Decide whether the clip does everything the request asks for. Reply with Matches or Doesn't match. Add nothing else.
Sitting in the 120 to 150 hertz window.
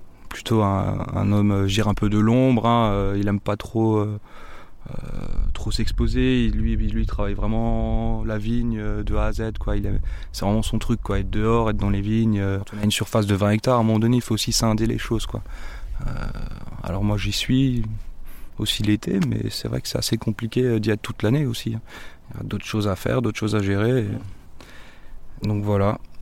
Doesn't match